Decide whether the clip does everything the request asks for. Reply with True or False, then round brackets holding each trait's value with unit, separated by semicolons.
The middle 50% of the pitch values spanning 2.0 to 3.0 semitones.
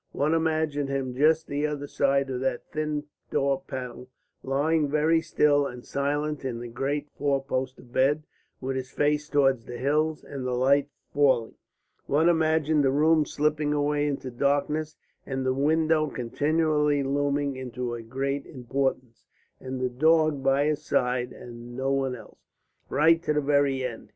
True (2.4 semitones)